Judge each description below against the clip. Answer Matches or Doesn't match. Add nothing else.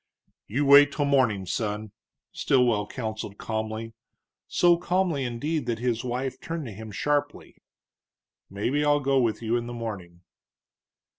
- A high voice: Doesn't match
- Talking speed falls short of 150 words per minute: Matches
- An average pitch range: Matches